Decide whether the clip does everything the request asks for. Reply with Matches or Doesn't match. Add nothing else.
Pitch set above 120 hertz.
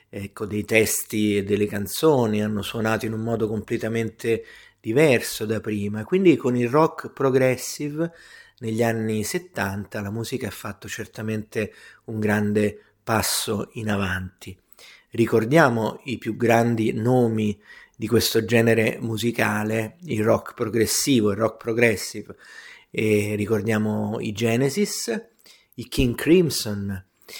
Doesn't match